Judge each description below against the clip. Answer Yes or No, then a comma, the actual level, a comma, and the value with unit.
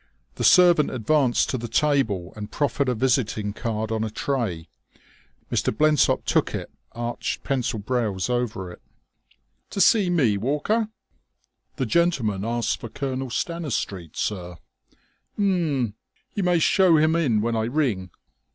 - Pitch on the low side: Yes, low, 125 Hz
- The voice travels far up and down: Yes, wide, 6.1 semitones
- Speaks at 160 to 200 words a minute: No, average, 140 wpm